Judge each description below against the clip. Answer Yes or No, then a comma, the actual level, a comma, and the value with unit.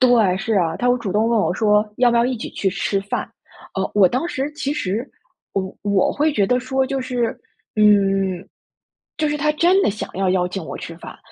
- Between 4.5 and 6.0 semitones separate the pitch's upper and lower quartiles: Yes, average, 4.8 semitones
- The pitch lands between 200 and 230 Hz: Yes, high, 215 Hz